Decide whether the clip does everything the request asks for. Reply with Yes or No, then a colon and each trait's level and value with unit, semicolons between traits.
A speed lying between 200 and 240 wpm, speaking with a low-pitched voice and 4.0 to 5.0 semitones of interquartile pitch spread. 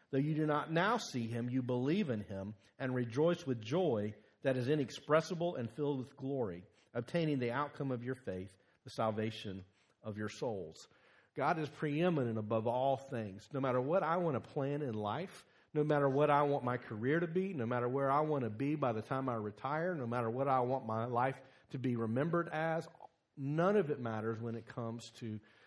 Yes: fast, 205 wpm; low, 130 Hz; average, 4.5 semitones